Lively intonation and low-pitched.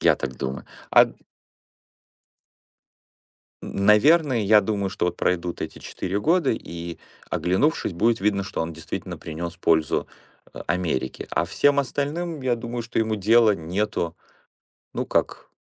Yes: wide, 5.8 semitones; low, 100 Hz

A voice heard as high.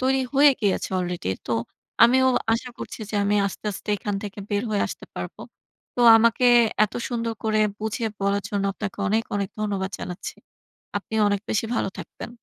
Yes: high, 210 Hz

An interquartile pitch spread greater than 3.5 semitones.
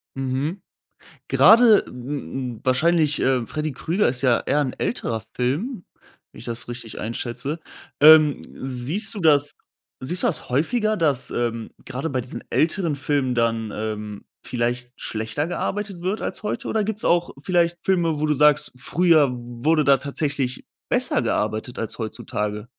Yes: wide, 5.5 semitones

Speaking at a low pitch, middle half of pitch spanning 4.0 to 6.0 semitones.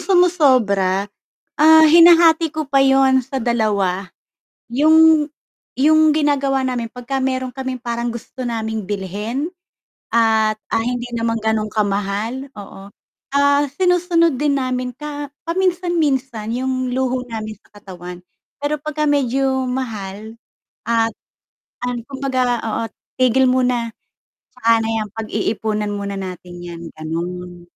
No: very high, 250 Hz; average, 4.6 semitones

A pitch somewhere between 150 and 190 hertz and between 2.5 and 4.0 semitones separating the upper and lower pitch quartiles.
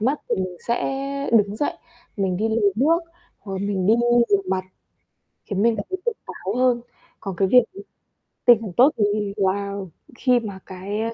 No: high, 210 Hz; average, 3.7 semitones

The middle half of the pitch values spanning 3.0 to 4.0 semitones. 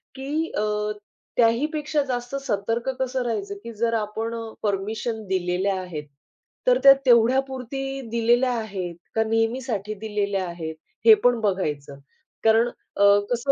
Yes: average, 3.7 semitones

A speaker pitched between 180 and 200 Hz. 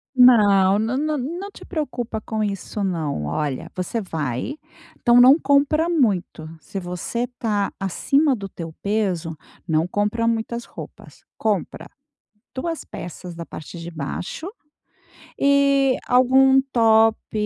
No: high, 220 Hz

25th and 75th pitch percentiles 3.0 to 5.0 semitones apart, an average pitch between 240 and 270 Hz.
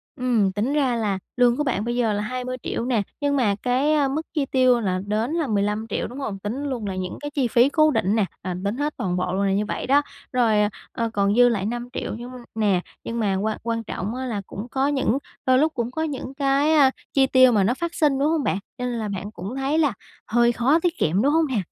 Yes: average, 4.5 semitones; high, 245 Hz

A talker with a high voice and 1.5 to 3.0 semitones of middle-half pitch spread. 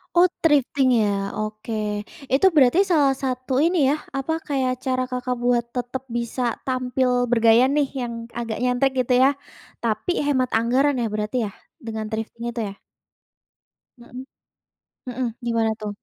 Yes: very high, 250 Hz; narrow, 2.5 semitones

